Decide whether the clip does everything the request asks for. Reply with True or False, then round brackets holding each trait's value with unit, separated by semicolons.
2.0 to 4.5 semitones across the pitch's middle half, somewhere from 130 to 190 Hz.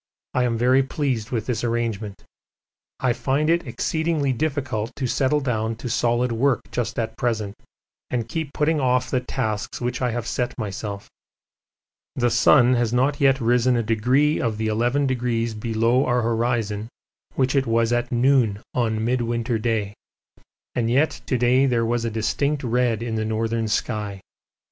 False (2.4 semitones; 120 Hz)